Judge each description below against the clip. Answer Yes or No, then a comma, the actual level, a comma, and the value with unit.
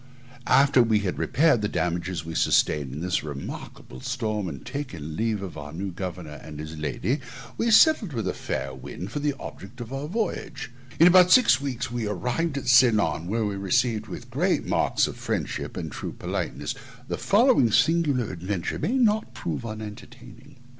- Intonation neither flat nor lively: No, wide, 7.8 semitones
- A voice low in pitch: Yes, low, 110 Hz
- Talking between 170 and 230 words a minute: Yes, average, 180 wpm